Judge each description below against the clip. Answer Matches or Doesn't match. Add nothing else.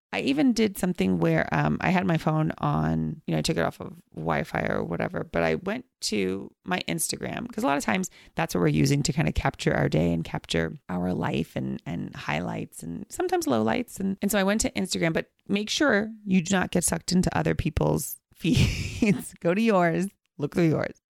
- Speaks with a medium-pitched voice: Matches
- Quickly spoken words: Matches